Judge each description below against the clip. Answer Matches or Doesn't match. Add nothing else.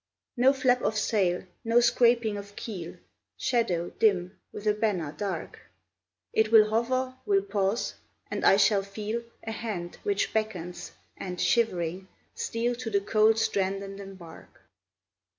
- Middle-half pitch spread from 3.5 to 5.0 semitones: Doesn't match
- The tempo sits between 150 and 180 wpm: Doesn't match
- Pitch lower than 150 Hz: Doesn't match